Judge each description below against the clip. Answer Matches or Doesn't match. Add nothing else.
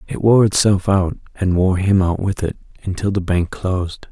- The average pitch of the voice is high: Doesn't match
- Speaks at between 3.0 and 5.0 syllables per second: Matches